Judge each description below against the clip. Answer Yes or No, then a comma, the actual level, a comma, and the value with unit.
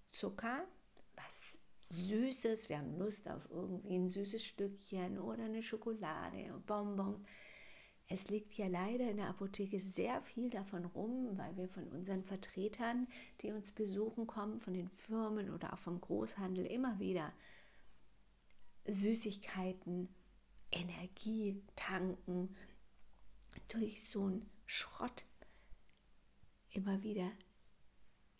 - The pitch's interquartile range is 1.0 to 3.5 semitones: Yes, average, 3.0 semitones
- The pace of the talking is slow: Yes, slow, 110 wpm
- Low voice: No, high, 200 Hz